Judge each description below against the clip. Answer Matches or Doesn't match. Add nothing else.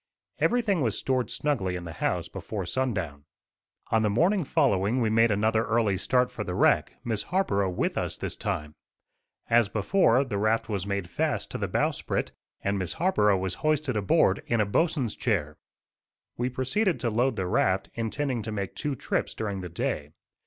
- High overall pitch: Doesn't match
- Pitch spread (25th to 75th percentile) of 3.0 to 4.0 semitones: Doesn't match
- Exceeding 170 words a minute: Matches